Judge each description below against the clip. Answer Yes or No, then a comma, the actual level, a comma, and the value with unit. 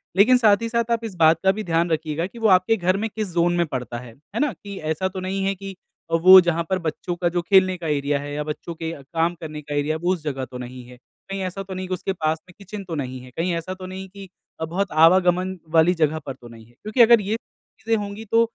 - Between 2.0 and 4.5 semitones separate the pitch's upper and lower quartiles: Yes, average, 3.8 semitones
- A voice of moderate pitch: Yes, medium, 180 Hz